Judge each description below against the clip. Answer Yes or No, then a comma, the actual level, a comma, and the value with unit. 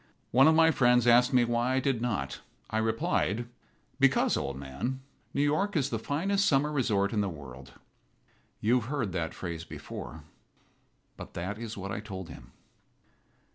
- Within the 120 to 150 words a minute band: No, average, 170 wpm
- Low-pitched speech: Yes, low, 120 Hz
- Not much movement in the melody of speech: No, wide, 5.6 semitones